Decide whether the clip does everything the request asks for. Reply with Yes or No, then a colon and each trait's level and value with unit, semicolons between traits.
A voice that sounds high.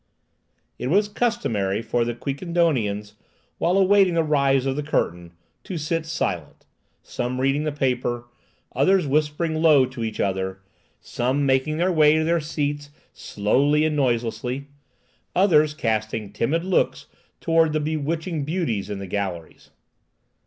No: medium, 145 Hz